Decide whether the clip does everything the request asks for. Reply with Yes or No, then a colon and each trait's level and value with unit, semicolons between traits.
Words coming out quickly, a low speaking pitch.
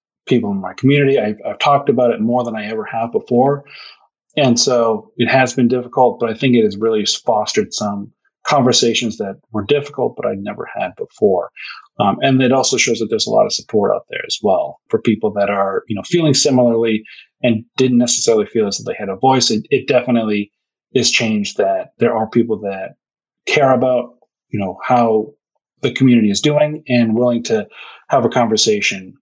No: average, 195 wpm; low, 120 Hz